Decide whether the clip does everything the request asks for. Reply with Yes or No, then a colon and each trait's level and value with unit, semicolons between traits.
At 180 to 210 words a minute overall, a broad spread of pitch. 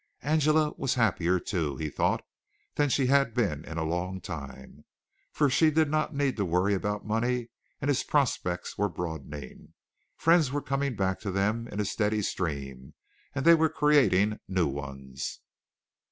No: average, 165 wpm; wide, 8.9 semitones